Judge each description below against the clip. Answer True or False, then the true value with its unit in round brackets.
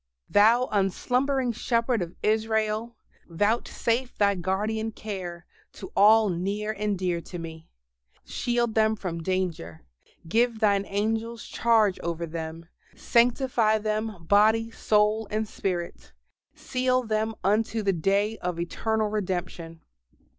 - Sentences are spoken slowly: True (120 wpm)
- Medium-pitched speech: False (210 Hz)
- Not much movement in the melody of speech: False (3.3 semitones)